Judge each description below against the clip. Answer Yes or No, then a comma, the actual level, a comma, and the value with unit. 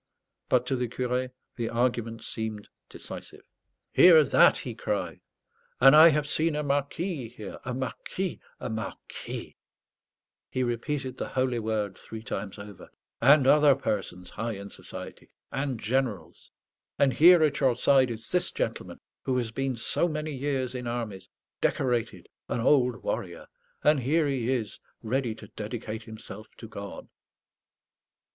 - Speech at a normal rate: Yes, average, 145 wpm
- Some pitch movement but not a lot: Yes, average, 3.9 semitones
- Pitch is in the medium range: No, low, 125 Hz